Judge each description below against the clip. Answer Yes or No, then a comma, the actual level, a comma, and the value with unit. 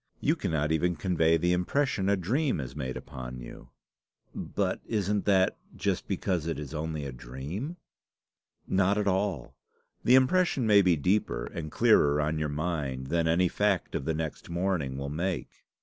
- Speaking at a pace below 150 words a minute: No, average, 165 wpm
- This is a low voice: Yes, very low, 85 Hz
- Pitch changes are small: No, average, 4.8 semitones